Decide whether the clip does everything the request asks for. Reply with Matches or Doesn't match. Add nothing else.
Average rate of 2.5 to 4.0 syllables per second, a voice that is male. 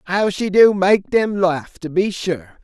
Matches